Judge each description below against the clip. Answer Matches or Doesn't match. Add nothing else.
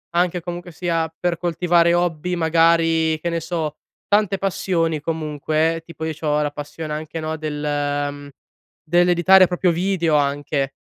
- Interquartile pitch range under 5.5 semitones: Matches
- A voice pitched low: Doesn't match